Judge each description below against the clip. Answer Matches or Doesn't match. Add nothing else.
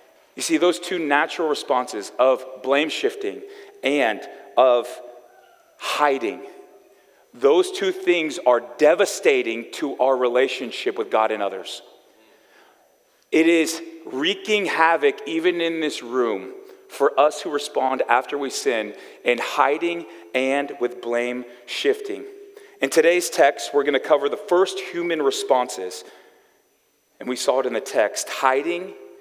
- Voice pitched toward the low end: Doesn't match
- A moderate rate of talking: Doesn't match